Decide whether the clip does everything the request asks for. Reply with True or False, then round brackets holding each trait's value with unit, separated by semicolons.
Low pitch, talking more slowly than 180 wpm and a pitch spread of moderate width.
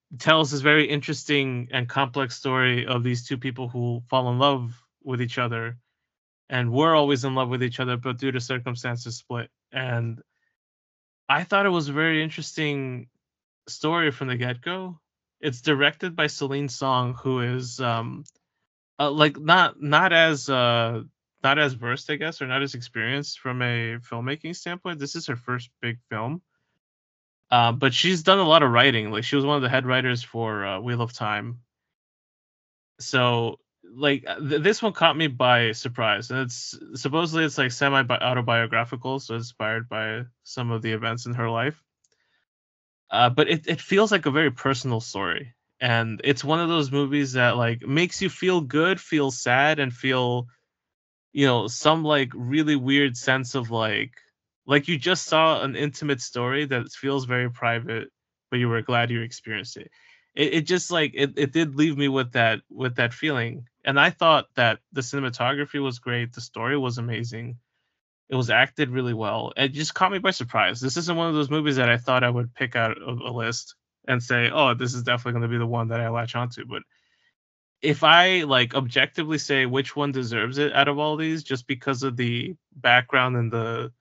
False (130 Hz; 190 wpm; 3.5 semitones)